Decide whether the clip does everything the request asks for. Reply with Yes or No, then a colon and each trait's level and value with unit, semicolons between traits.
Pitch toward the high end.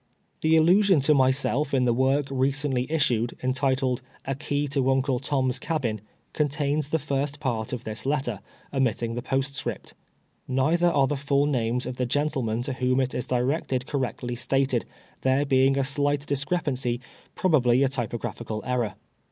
No: low, 135 Hz